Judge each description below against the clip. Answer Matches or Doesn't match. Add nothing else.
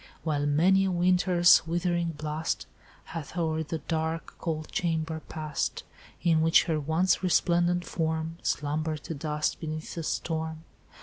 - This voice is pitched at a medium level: Matches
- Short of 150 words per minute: Matches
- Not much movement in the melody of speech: Matches